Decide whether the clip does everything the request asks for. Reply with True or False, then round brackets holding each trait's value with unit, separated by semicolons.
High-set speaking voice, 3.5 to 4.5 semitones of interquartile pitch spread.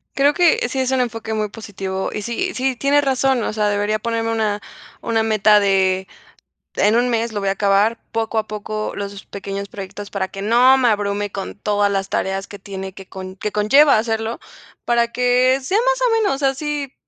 True (220 Hz; 3.9 semitones)